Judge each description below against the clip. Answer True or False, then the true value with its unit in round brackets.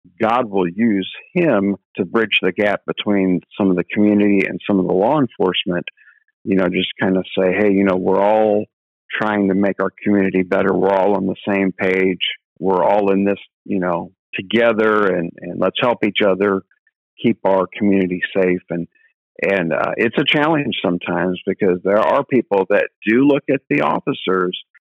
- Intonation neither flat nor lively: False (1.8 semitones)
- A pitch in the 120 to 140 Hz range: False (95 Hz)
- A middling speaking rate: True (185 wpm)